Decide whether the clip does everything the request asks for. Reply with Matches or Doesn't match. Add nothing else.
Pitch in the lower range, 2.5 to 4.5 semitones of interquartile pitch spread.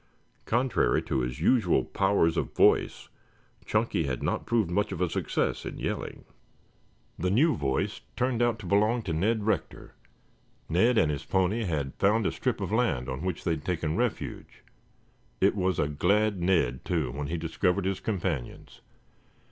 Doesn't match